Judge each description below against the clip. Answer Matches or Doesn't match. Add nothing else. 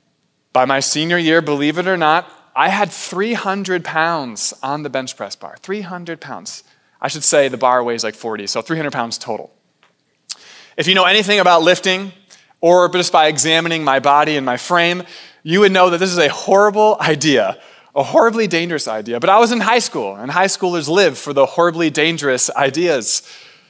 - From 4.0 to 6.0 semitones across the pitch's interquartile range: Matches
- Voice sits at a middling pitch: Matches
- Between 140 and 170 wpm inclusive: Doesn't match